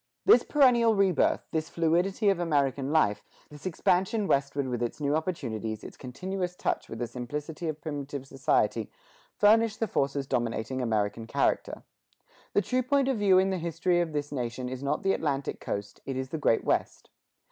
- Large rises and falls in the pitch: Yes, wide, 6.3 semitones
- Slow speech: No, average, 175 wpm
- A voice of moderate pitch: Yes, medium, 150 Hz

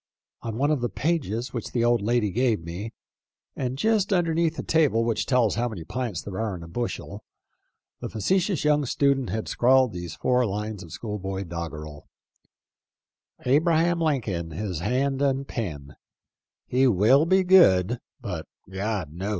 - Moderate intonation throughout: No, wide, 6.3 semitones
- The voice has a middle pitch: No, low, 115 Hz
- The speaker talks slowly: No, average, 165 wpm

